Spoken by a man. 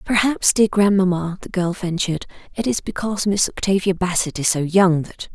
No: female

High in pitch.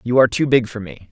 No: low, 115 Hz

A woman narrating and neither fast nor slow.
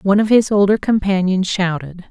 Yes: female; average, 170 wpm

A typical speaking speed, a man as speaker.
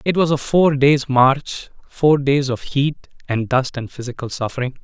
Yes: average, 175 wpm; male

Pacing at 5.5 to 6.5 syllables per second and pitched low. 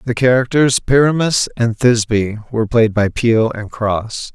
No: 4.8 syllables/s; low, 115 Hz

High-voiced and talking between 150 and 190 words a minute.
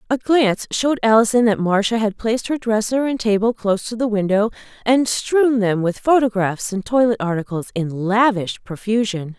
Yes: high, 220 Hz; average, 175 wpm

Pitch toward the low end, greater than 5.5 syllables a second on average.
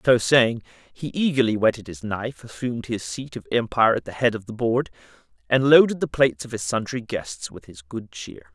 No: low, 115 Hz; 5.4 syllables/s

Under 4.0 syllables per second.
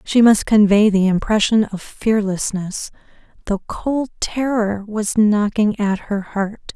Yes: 3.8 syllables/s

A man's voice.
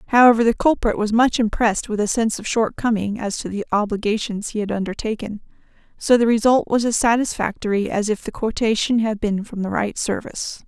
No: female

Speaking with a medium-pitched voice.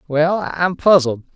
Yes: medium, 160 Hz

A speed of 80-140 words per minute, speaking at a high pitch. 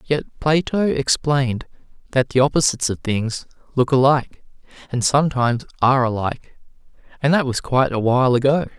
No: slow, 135 wpm; low, 135 Hz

